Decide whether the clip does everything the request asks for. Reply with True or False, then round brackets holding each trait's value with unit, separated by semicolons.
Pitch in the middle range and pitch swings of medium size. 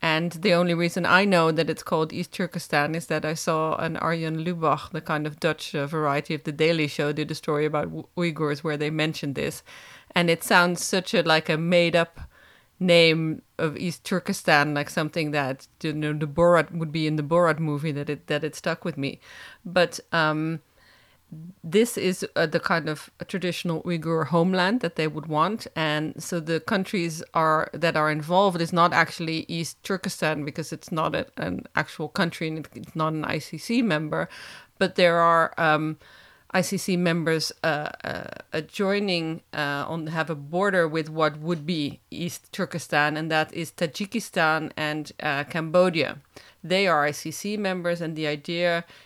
False (165 Hz; 2.2 semitones)